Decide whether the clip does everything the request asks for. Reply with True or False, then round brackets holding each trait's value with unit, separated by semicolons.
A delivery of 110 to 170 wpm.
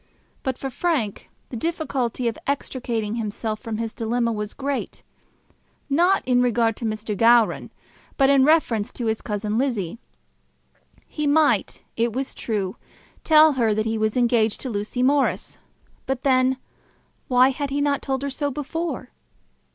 True (150 wpm)